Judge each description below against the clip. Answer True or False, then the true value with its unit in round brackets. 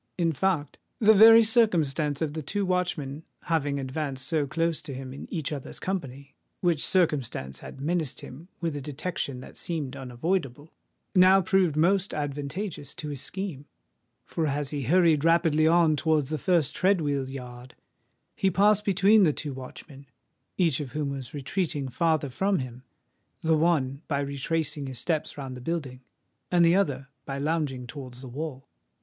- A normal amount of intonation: True (4.1 semitones)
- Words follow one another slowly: False (160 wpm)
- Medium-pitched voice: True (150 Hz)